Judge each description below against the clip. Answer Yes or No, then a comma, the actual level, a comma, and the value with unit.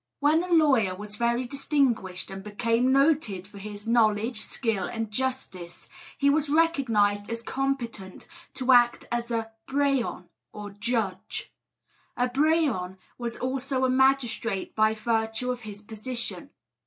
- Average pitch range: Yes, average, 4.1 semitones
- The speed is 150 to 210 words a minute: No, slow, 135 wpm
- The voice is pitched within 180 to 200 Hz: No, high, 235 Hz